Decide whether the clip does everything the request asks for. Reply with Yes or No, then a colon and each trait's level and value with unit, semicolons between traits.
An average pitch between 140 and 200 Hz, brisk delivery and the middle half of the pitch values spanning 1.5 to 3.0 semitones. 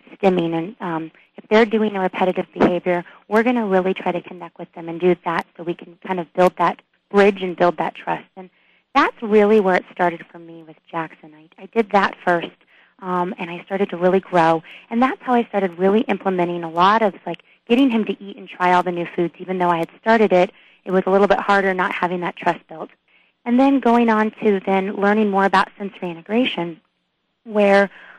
Yes: medium, 185 Hz; fast, 225 wpm; average, 2.7 semitones